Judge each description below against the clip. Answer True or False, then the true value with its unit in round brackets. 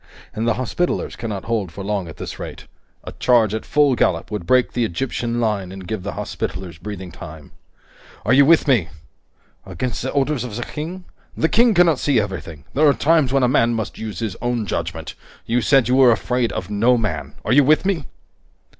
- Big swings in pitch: False (4.9 semitones)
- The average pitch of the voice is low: True (120 Hz)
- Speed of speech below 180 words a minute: False (205 wpm)